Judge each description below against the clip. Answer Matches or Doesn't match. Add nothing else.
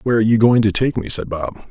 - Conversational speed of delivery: Doesn't match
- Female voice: Doesn't match